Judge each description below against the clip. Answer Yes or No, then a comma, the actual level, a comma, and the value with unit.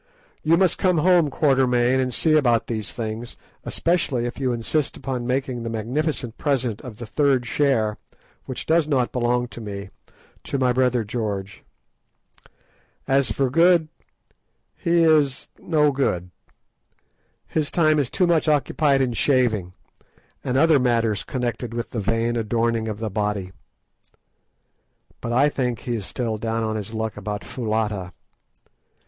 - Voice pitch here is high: No, low, 125 Hz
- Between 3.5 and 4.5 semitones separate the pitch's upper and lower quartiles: Yes, average, 4.2 semitones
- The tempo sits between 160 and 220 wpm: No, average, 145 wpm